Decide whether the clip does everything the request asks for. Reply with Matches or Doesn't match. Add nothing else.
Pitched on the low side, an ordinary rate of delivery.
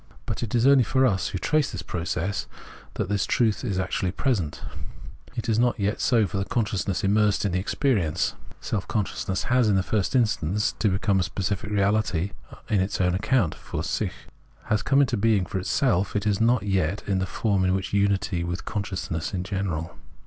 Matches